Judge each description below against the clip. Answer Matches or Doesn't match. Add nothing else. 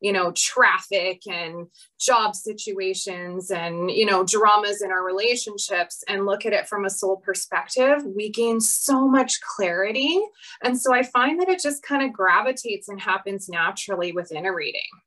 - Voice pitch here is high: Matches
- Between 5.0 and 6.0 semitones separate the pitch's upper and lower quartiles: Doesn't match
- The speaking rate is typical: Matches